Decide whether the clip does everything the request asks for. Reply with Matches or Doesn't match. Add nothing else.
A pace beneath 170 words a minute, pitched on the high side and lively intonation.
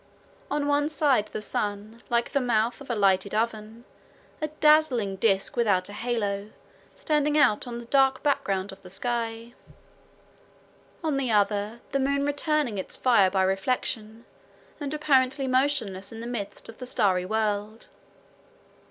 Doesn't match